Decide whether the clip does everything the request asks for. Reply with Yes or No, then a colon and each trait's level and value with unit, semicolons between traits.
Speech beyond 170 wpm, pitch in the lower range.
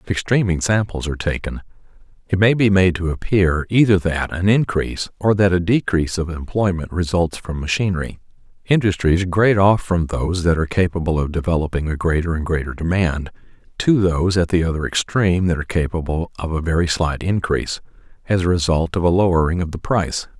Yes: average, 180 wpm; very low, 90 Hz